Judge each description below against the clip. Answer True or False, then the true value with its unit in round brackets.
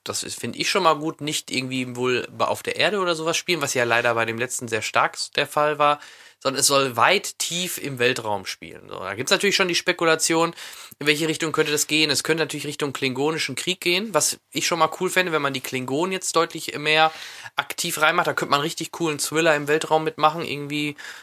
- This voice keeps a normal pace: False (225 wpm)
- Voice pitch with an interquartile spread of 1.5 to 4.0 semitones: True (3.0 semitones)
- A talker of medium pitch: True (155 Hz)